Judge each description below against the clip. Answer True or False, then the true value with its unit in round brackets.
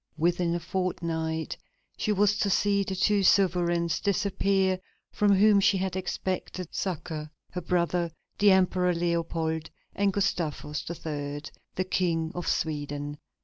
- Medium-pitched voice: True (180 Hz)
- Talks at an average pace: False (130 wpm)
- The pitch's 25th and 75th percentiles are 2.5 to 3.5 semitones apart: True (2.8 semitones)